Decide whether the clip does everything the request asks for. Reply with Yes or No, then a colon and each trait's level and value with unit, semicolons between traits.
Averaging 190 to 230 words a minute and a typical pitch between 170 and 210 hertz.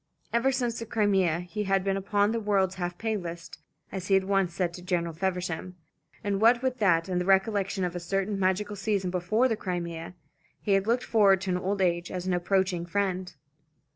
Yes: average, 200 wpm; high, 190 Hz